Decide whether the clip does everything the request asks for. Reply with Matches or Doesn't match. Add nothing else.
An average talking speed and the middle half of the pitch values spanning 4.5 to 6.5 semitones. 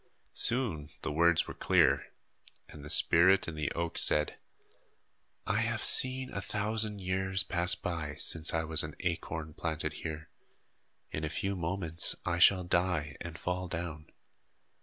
Doesn't match